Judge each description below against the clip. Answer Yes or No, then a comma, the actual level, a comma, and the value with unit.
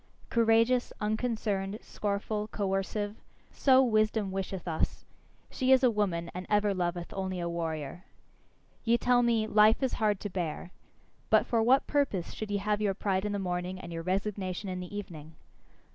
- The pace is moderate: Yes, average, 165 wpm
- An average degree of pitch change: Yes, average, 3.2 semitones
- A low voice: No, high, 205 Hz